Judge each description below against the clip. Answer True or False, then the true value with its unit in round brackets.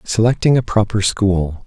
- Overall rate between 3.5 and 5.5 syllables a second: True (4.5 syllables/s)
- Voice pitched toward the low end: True (105 Hz)